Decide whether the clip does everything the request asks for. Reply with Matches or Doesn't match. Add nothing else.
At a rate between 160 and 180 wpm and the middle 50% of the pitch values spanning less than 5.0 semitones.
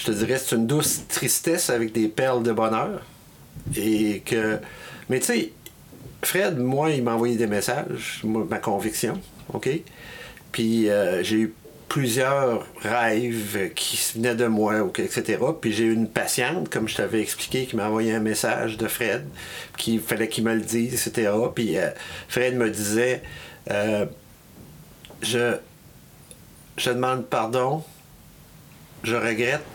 Doesn't match